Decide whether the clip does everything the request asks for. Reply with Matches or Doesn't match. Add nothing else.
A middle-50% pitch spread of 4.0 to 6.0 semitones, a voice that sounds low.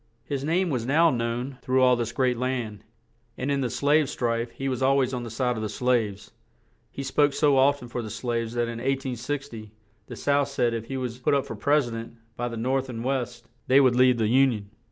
Doesn't match